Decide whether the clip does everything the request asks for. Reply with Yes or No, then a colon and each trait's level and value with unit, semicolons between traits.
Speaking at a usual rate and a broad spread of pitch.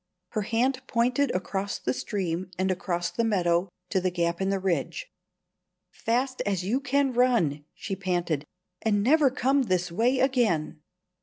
Yes: average, 155 wpm; wide, 6.1 semitones